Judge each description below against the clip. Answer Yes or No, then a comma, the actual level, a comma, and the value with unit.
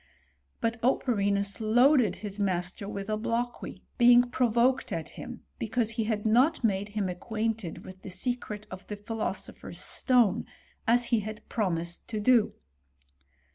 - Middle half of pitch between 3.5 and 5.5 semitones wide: No, average, 3.1 semitones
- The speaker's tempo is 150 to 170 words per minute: No, average, 140 wpm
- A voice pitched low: No, high, 220 Hz